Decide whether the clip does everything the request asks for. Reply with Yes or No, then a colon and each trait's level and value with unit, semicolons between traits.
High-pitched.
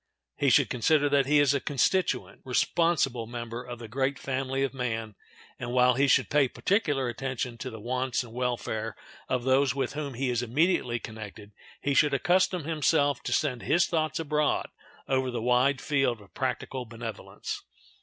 No: low, 130 Hz